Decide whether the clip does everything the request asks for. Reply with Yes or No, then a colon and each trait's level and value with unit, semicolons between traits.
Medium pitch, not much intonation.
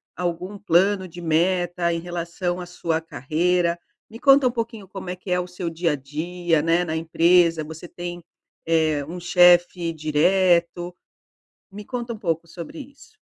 Yes: medium, 175 Hz; narrow, 1.7 semitones